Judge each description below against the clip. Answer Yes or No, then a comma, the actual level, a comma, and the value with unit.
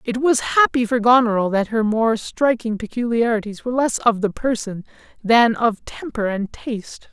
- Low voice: No, high, 230 Hz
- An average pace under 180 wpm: Yes, average, 170 wpm